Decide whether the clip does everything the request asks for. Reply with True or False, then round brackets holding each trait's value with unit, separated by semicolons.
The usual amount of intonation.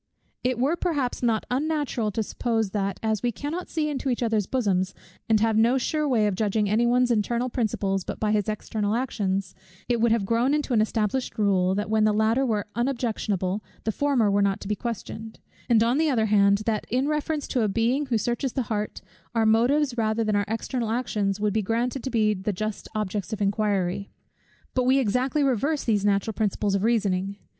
True (3.3 semitones)